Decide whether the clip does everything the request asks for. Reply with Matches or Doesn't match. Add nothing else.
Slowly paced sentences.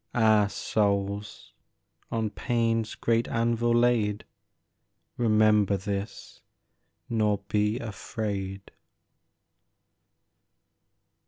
Matches